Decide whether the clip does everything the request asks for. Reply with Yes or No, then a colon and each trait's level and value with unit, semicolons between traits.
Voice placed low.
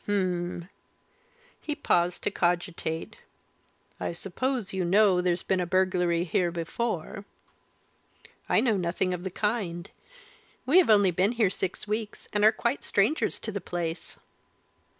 No: medium, 185 Hz